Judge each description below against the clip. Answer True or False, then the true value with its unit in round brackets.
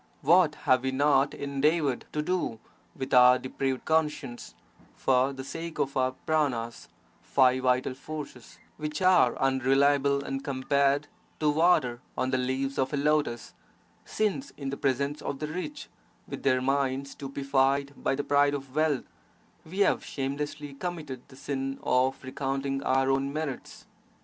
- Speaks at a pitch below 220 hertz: True (140 Hz)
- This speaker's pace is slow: False (150 wpm)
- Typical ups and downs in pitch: False (2.1 semitones)